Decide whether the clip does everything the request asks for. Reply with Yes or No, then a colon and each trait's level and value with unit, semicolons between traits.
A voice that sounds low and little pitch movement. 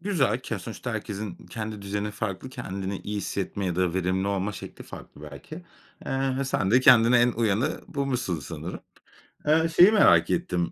No: low, 105 Hz; average, 5.3 semitones